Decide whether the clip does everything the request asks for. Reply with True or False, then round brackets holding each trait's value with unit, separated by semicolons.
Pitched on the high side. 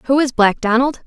True (250 Hz)